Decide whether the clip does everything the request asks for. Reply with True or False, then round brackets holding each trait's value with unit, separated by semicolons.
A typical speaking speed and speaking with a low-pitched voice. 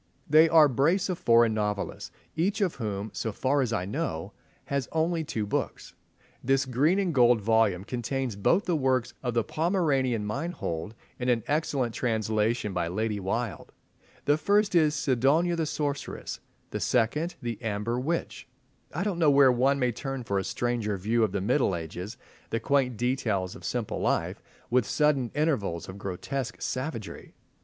True (165 wpm; 125 Hz)